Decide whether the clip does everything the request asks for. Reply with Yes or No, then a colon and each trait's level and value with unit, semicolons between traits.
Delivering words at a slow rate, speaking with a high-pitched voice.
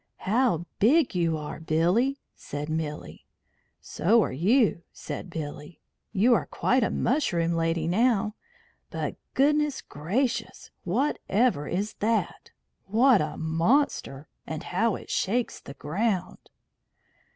Yes: slow, 120 wpm; high, 195 Hz